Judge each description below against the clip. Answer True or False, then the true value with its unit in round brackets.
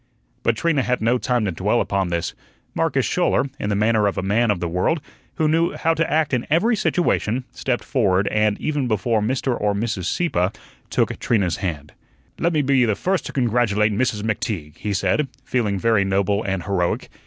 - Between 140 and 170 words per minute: False (195 wpm)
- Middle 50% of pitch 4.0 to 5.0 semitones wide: True (4.7 semitones)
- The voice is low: True (110 Hz)